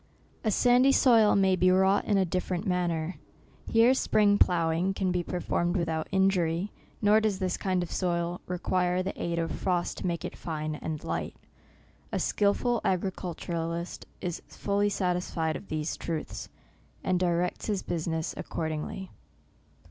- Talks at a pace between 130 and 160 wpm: Yes, average, 155 wpm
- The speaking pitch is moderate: Yes, medium, 180 Hz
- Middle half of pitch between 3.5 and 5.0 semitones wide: No, narrow, 2.4 semitones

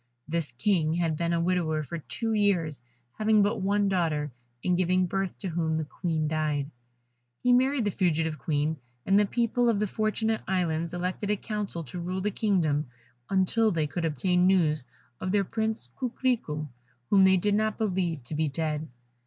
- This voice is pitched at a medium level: Yes, medium, 180 Hz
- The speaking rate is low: No, average, 180 wpm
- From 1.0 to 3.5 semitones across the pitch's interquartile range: No, average, 4.6 semitones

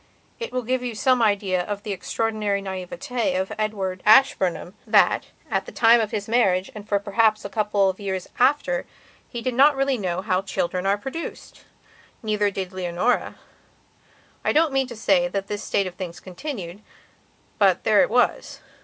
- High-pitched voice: Yes, high, 210 Hz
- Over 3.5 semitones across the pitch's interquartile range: Yes, average, 4.3 semitones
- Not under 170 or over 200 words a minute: Yes, average, 175 wpm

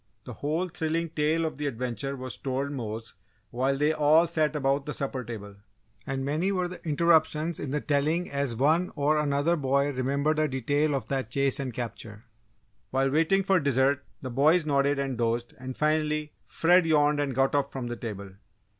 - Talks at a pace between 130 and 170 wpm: No, average, 185 wpm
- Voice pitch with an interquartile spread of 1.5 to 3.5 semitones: Yes, average, 2.8 semitones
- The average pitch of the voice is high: No, medium, 140 Hz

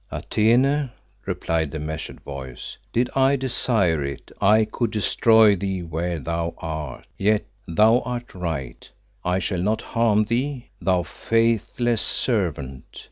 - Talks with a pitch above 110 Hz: No, low, 100 Hz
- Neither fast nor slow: No, slow, 130 wpm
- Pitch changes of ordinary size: No, wide, 6.1 semitones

